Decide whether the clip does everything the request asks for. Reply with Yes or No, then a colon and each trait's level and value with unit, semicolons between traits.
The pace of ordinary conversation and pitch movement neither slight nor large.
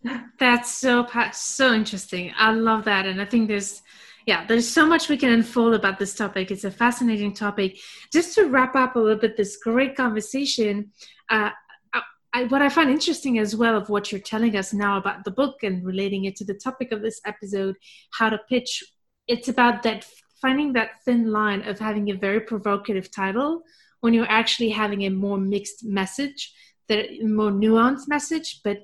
Yes: average, 185 wpm; average, 3.4 semitones